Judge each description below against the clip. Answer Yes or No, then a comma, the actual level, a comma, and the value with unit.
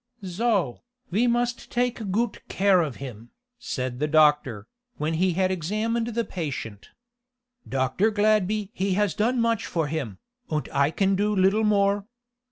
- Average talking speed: Yes, average, 150 wpm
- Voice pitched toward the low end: No, high, 190 Hz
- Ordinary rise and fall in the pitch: No, wide, 6.1 semitones